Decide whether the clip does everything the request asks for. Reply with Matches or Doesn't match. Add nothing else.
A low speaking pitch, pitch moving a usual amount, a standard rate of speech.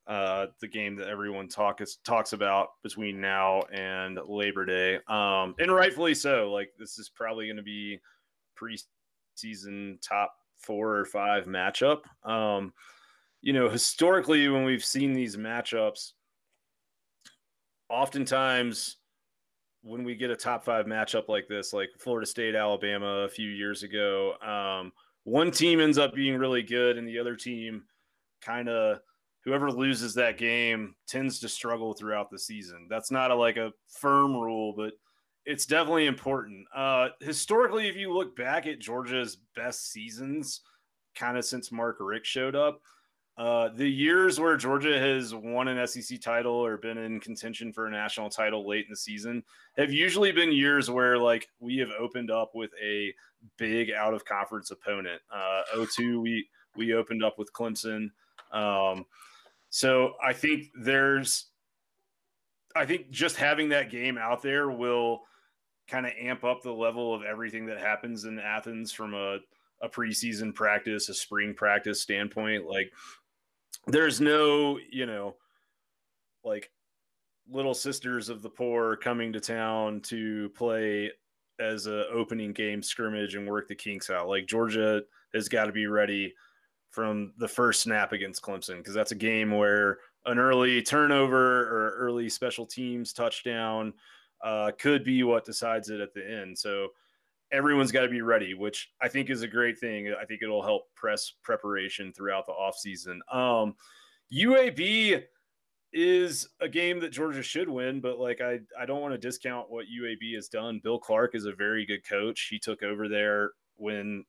Matches